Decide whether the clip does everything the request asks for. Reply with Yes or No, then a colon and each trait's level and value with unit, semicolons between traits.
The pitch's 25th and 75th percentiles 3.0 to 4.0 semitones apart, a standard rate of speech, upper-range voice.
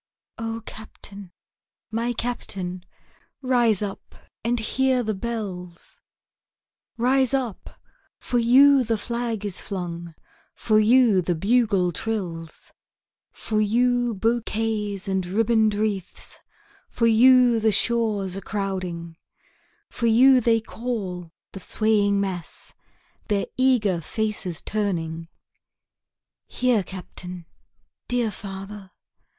No: average, 3.7 semitones; slow, 100 wpm; high, 215 Hz